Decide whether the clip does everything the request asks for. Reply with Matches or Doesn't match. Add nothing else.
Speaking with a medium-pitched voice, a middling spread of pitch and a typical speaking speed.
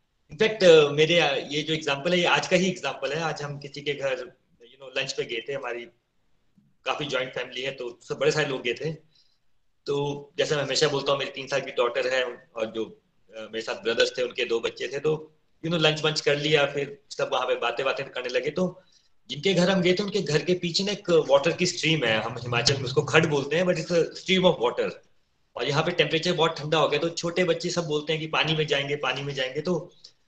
Doesn't match